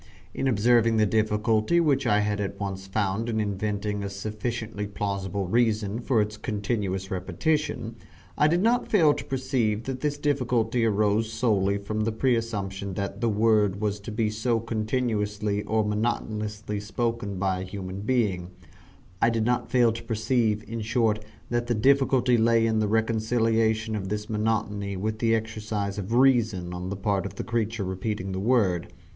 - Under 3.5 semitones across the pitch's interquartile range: Yes, narrow, 2.4 semitones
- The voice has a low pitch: Yes, low, 110 Hz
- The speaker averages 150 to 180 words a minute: Yes, average, 165 wpm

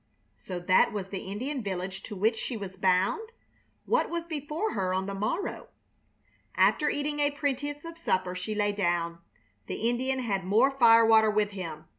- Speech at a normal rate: Yes, average, 170 wpm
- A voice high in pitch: Yes, high, 215 Hz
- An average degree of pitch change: No, wide, 7.1 semitones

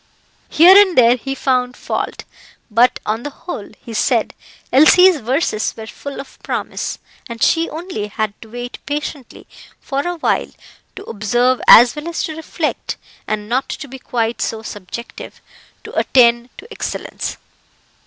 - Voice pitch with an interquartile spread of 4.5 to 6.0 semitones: Yes, average, 5.0 semitones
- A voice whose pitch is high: Yes, very high, 250 Hz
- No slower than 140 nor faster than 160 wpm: Yes, average, 150 wpm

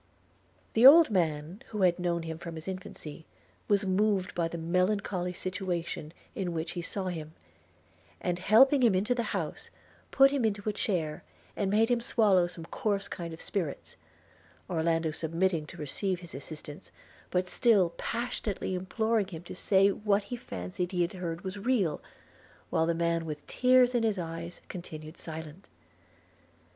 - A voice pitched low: No, medium, 180 Hz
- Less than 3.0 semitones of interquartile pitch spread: No, average, 3.9 semitones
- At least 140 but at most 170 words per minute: Yes, average, 165 wpm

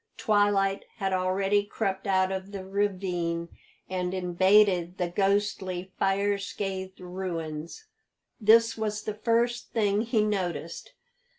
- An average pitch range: No, narrow, 2.0 semitones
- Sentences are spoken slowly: Yes, slow, 115 wpm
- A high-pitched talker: Yes, high, 195 Hz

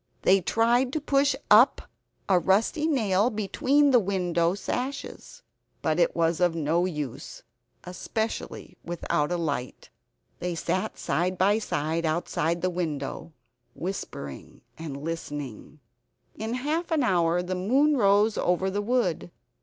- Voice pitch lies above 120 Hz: Yes, medium, 185 Hz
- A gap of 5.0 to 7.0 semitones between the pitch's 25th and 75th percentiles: Yes, average, 5.3 semitones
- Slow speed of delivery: Yes, slow, 130 wpm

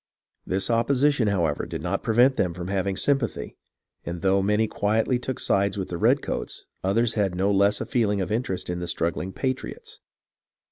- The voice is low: Yes, low, 100 Hz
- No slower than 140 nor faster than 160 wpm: No, average, 180 wpm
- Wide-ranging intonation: No, average, 3.7 semitones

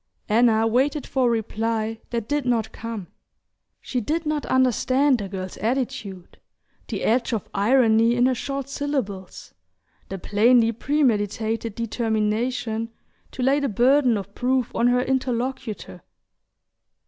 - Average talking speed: No, slow, 130 wpm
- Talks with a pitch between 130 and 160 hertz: No, high, 235 Hz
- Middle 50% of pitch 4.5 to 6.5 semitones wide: No, average, 3.0 semitones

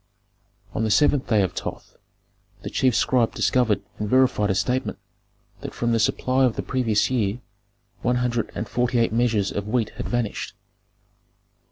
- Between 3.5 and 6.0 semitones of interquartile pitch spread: No, average, 3.0 semitones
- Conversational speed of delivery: Yes, average, 165 wpm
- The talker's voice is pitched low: Yes, low, 120 Hz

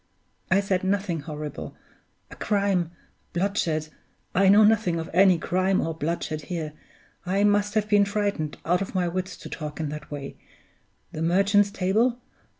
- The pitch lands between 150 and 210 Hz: Yes, medium, 185 Hz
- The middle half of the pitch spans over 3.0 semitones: Yes, average, 3.8 semitones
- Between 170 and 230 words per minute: No, average, 155 wpm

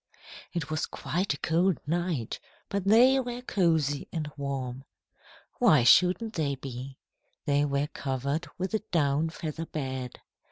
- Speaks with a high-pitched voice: No, medium, 155 Hz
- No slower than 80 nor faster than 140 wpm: Yes, slow, 135 wpm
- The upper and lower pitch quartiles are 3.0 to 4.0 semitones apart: No, average, 4.7 semitones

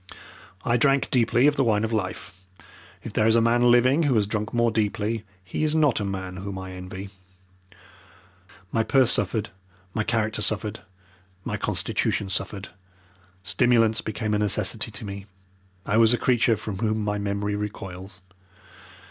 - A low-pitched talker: Yes, low, 110 Hz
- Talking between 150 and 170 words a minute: Yes, average, 160 wpm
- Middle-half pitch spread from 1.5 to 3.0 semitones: Yes, average, 2.7 semitones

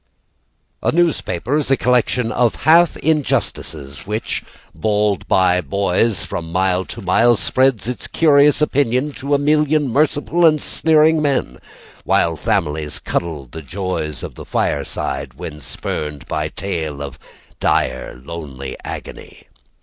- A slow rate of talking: Yes, slow, 130 wpm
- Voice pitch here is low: Yes, low, 105 Hz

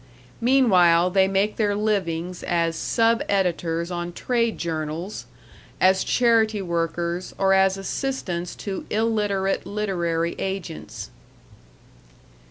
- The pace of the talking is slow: Yes, slow, 100 wpm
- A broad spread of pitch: No, average, 3.7 semitones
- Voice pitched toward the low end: No, high, 190 Hz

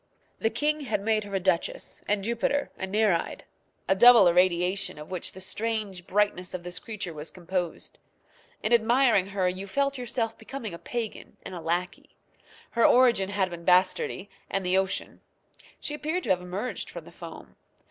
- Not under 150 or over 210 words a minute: Yes, average, 175 wpm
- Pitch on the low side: No, high, 195 Hz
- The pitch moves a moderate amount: Yes, average, 4.1 semitones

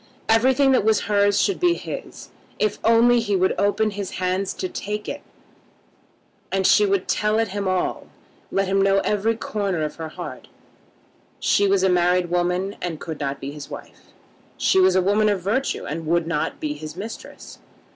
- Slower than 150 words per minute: No, average, 185 wpm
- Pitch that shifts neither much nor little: Yes, average, 3.0 semitones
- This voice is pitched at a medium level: No, high, 195 Hz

